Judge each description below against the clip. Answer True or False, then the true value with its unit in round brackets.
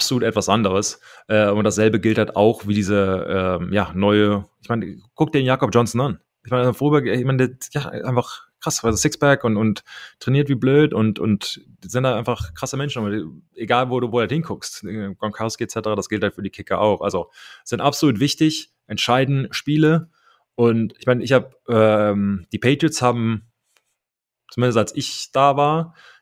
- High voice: False (120 Hz)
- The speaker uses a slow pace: False (185 wpm)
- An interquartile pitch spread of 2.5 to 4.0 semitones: False (4.4 semitones)